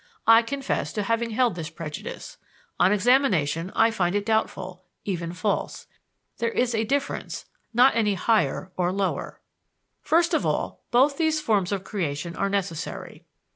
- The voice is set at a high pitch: Yes, high, 210 Hz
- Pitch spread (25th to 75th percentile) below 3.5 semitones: No, average, 4.6 semitones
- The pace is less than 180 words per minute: Yes, average, 150 wpm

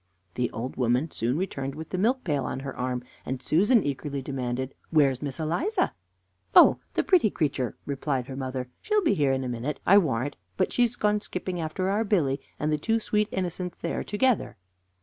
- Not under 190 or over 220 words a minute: Yes, fast, 205 wpm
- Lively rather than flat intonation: Yes, wide, 6.9 semitones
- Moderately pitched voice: Yes, medium, 150 Hz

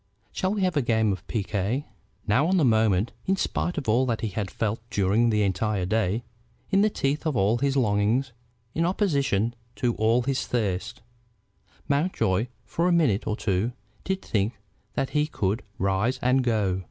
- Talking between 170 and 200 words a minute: Yes, average, 175 wpm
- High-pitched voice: No, low, 115 Hz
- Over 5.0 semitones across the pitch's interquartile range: Yes, wide, 5.4 semitones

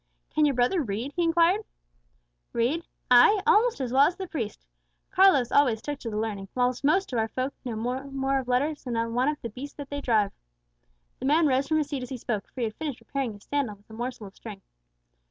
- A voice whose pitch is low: No, very high, 260 Hz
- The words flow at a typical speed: No, fast, 230 wpm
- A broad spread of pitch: No, average, 4.1 semitones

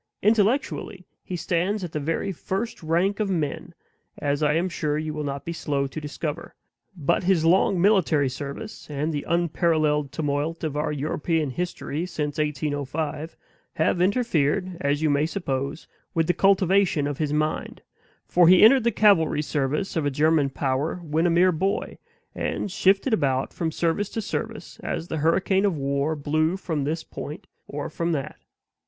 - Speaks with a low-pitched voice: No, medium, 160 Hz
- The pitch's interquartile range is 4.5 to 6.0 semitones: No, average, 3.9 semitones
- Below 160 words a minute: No, average, 170 wpm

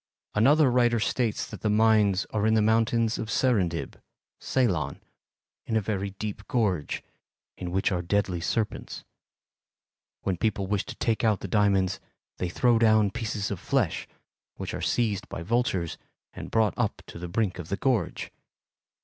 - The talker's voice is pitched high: No, low, 105 Hz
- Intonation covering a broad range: No, average, 3.1 semitones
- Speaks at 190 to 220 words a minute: No, average, 160 wpm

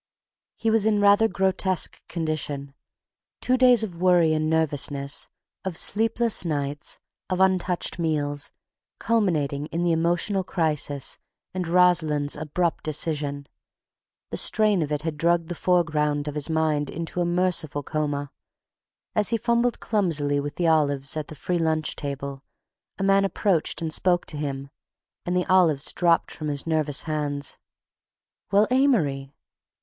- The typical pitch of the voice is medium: Yes, medium, 160 Hz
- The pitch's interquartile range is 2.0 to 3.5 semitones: No, average, 4.0 semitones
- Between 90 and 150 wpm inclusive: Yes, average, 140 wpm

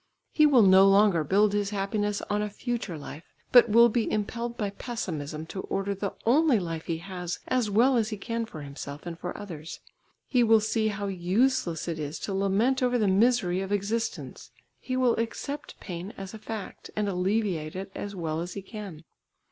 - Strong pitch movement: No, average, 4.2 semitones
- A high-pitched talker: Yes, high, 200 Hz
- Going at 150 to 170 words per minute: No, average, 195 wpm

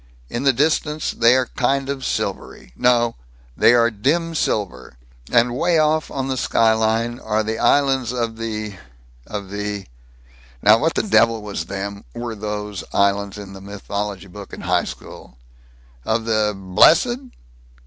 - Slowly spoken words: No, average, 150 wpm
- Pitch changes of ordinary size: Yes, average, 4.2 semitones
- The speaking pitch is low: Yes, low, 110 Hz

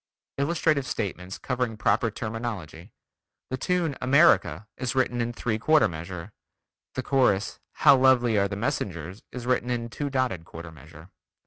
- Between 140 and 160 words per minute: Yes, average, 145 wpm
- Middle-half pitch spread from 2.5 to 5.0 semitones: No, wide, 5.4 semitones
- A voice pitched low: Yes, low, 115 Hz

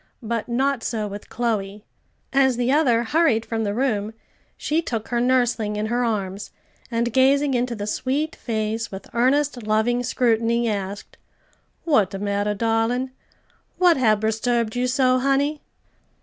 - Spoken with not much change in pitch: No, average, 3.2 semitones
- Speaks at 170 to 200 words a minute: No, average, 150 wpm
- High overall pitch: Yes, high, 235 Hz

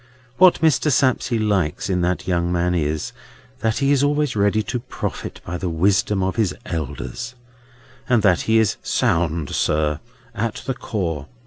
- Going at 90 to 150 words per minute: No, average, 160 wpm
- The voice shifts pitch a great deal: Yes, wide, 5.8 semitones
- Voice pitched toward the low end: Yes, low, 100 Hz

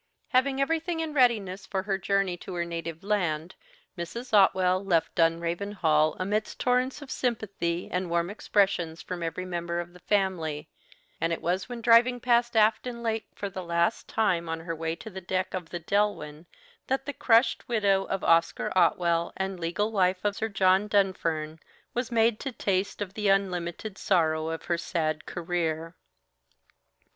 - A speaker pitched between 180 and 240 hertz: Yes, high, 190 Hz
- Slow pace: No, average, 170 wpm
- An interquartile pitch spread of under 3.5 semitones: No, average, 4.1 semitones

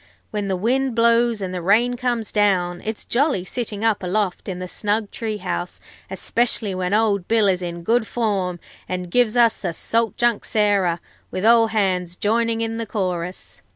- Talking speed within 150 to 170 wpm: No, average, 180 wpm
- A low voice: No, high, 210 Hz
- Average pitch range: Yes, average, 3.8 semitones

